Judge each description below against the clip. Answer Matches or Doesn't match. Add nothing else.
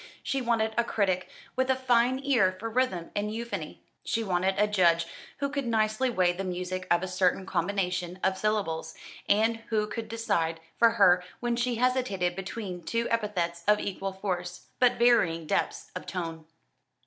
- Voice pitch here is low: Doesn't match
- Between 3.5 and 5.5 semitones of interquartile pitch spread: Matches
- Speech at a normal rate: Matches